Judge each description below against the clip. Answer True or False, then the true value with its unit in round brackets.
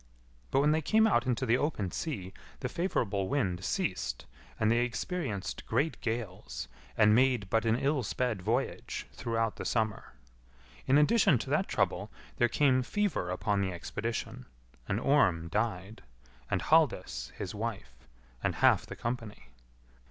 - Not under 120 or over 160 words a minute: True (150 wpm)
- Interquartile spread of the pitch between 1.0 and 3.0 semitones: False (5.2 semitones)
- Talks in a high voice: False (115 Hz)